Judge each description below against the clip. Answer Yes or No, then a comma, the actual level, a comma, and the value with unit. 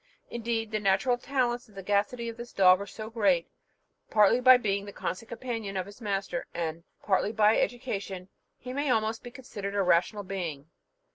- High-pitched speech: Yes, high, 210 Hz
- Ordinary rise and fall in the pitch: Yes, average, 3.4 semitones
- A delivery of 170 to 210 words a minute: Yes, average, 185 wpm